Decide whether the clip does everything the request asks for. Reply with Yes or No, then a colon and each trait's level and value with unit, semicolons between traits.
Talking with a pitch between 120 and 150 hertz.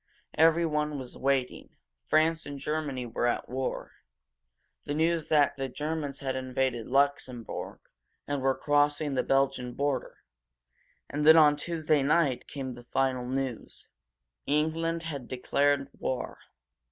Yes: medium, 140 Hz